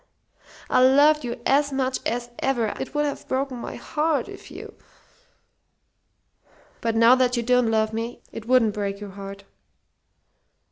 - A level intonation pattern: No, average, 3.3 semitones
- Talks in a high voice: Yes, high, 245 Hz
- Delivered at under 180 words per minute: Yes, average, 155 wpm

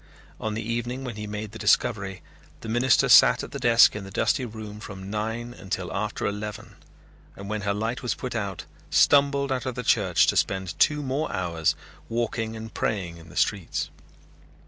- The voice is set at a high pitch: No, low, 110 Hz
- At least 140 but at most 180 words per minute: No, average, 190 wpm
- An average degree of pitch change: Yes, average, 3.3 semitones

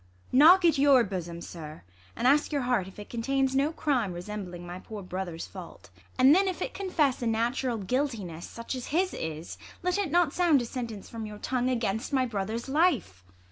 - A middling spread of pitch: No, wide, 6.6 semitones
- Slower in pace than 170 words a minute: No, average, 200 wpm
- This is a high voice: Yes, high, 240 Hz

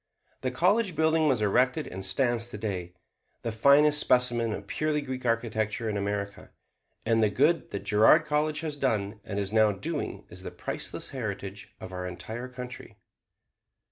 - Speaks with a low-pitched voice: Yes, low, 120 Hz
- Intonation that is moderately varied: No, wide, 6.0 semitones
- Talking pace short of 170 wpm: Yes, average, 160 wpm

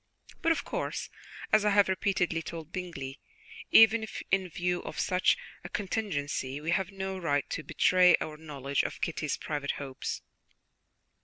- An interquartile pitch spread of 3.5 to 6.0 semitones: Yes, average, 4.7 semitones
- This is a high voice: No, medium, 175 Hz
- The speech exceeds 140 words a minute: Yes, average, 150 wpm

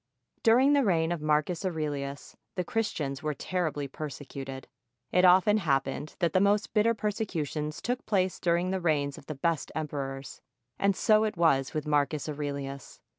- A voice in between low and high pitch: Yes, medium, 160 Hz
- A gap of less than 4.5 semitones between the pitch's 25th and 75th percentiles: No, average, 5.0 semitones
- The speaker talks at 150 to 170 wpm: Yes, average, 160 wpm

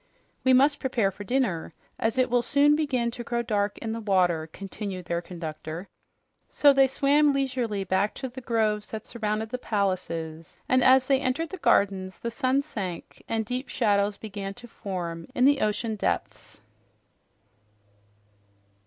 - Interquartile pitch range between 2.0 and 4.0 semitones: No, average, 4.8 semitones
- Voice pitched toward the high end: Yes, high, 220 Hz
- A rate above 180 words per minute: No, average, 160 wpm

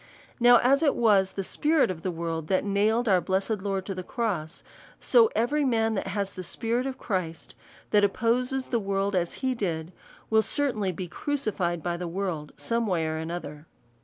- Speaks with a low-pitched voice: No, high, 200 Hz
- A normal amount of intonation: Yes, average, 4.8 semitones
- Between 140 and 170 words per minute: No, average, 190 wpm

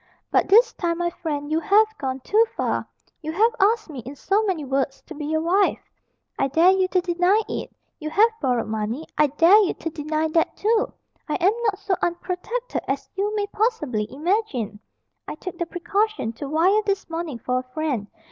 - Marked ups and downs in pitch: Yes, wide, 5.8 semitones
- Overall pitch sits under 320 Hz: No, very high, 340 Hz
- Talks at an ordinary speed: Yes, average, 195 wpm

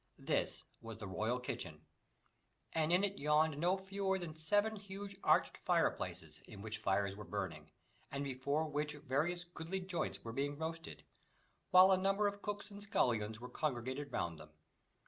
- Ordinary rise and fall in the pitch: No, wide, 7.2 semitones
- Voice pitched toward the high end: No, medium, 155 Hz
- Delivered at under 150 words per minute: No, average, 165 wpm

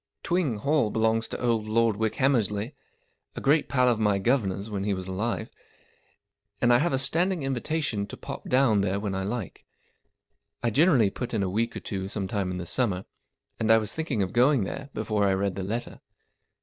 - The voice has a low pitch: Yes, low, 110 Hz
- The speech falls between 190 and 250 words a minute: Yes, average, 200 wpm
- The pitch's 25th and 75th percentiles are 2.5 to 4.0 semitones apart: No, average, 4.4 semitones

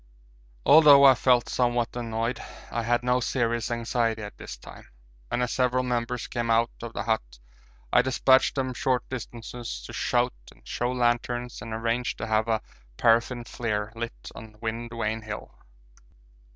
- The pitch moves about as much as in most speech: No, narrow, 1.5 semitones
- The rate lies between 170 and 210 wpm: No, average, 160 wpm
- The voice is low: Yes, low, 120 Hz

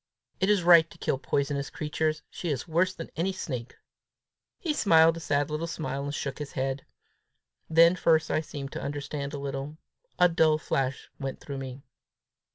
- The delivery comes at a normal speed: Yes, average, 175 wpm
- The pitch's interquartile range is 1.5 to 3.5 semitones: Yes, average, 3.0 semitones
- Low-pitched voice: No, medium, 150 Hz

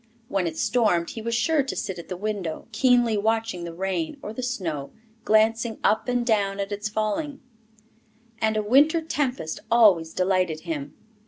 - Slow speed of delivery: No, average, 170 wpm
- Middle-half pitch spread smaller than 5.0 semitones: Yes, average, 4.6 semitones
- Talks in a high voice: Yes, high, 215 Hz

